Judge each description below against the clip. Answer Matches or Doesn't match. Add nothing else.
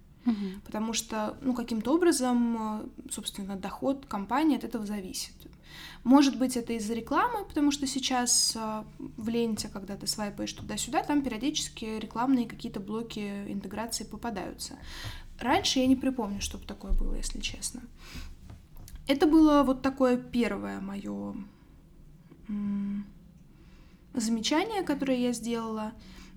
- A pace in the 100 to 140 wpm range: Matches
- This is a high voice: Matches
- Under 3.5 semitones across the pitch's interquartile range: Doesn't match